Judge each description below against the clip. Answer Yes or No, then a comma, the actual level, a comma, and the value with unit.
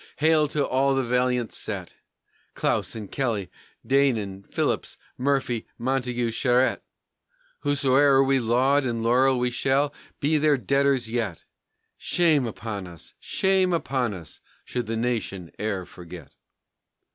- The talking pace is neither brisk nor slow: No, slow, 120 wpm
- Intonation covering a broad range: No, average, 3.5 semitones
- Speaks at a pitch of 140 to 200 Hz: No, low, 125 Hz